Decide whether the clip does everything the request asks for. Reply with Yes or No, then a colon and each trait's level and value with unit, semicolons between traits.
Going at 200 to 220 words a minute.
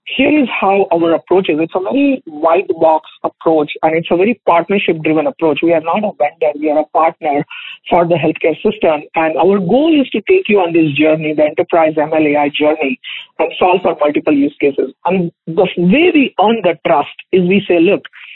Yes: fast, 205 wpm